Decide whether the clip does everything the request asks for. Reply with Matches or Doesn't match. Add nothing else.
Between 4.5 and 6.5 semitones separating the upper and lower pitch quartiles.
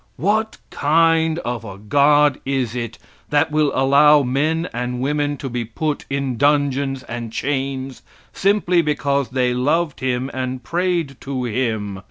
Doesn't match